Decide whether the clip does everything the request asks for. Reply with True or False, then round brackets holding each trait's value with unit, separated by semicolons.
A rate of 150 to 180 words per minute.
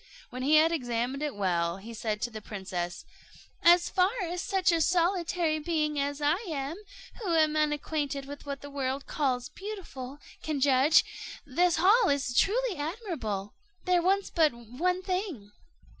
True (160 wpm)